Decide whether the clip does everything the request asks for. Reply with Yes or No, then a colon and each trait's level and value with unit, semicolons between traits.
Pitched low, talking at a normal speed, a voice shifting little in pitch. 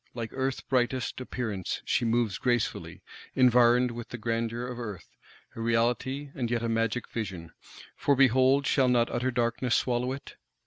Yes: low, 120 Hz; average, 155 wpm; narrow, 1.8 semitones